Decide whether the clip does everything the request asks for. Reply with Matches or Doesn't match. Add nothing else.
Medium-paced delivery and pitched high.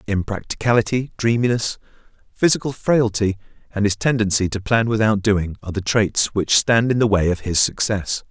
Doesn't match